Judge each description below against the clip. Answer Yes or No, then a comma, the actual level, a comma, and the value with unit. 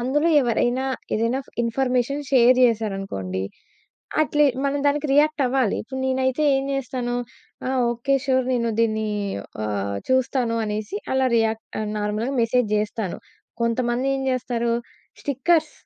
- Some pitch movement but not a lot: Yes, average, 3.1 semitones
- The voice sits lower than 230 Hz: No, very high, 250 Hz